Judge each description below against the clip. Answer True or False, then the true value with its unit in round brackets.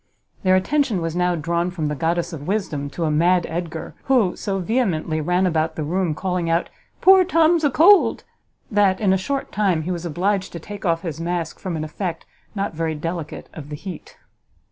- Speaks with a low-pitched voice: False (175 Hz)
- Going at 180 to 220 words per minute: True (200 wpm)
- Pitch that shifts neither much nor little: True (3.4 semitones)